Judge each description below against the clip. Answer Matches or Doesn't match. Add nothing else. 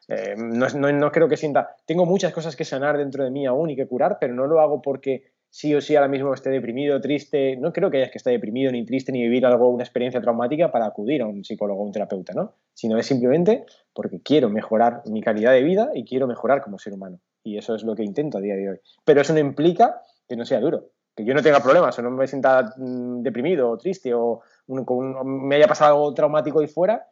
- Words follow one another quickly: Matches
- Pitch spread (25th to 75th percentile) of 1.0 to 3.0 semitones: Doesn't match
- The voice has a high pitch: Doesn't match